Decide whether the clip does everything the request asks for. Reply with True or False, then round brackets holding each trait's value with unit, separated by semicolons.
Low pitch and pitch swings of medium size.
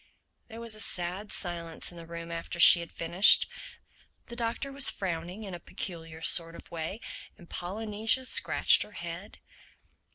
False (175 Hz; 4.2 semitones)